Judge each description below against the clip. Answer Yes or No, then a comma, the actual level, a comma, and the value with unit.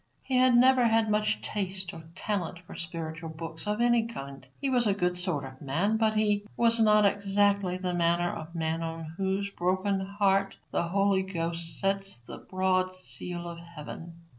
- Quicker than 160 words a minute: Yes, average, 180 wpm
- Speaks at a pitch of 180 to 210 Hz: Yes, high, 190 Hz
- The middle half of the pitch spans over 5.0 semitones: No, average, 3.6 semitones